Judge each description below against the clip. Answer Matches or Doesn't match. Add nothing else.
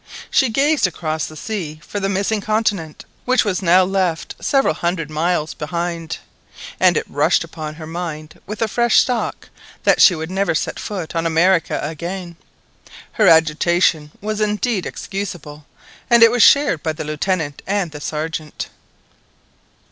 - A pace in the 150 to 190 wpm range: Matches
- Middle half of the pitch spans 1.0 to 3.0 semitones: Doesn't match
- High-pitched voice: Doesn't match